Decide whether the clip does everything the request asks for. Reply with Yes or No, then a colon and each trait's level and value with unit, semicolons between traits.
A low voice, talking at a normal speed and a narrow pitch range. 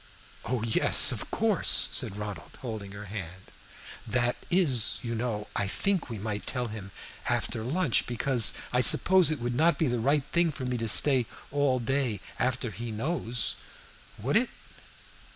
No: low, 120 Hz; average, 165 wpm; average, 4.3 semitones